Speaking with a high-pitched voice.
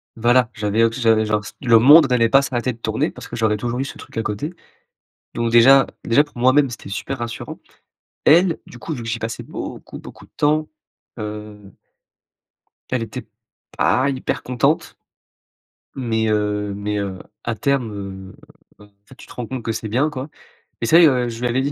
No: low, 115 Hz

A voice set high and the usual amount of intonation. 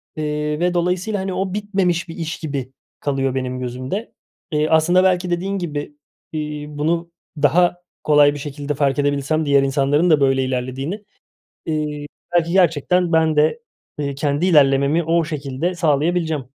No: medium, 155 Hz; average, 3.6 semitones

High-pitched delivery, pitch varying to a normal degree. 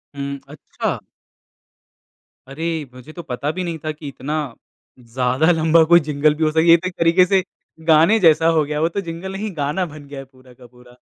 No: medium, 155 Hz; average, 3.2 semitones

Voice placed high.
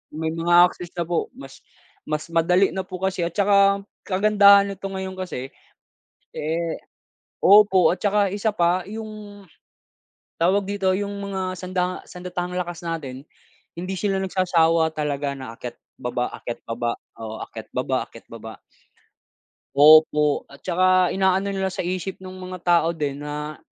No: medium, 180 Hz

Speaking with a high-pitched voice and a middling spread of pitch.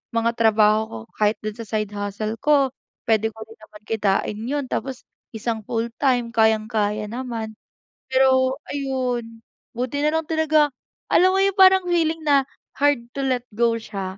Yes: high, 235 Hz; average, 4.3 semitones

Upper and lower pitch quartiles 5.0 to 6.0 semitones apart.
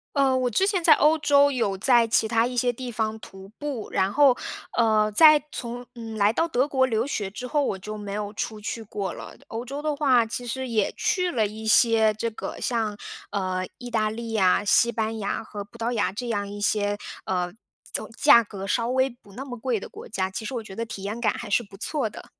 No: average, 3.4 semitones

